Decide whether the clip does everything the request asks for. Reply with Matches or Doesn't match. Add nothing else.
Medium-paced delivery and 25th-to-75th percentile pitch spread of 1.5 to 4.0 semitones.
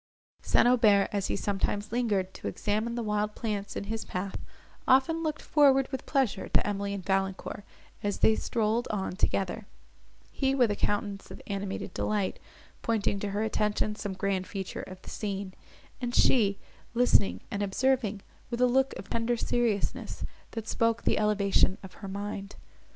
Matches